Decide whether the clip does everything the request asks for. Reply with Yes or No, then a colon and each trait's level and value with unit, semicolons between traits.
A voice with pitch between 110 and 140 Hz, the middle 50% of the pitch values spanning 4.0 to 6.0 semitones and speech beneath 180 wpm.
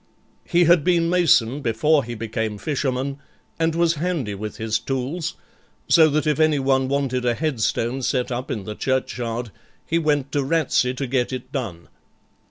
Yes: low, 135 Hz; average, 4.5 semitones; average, 165 wpm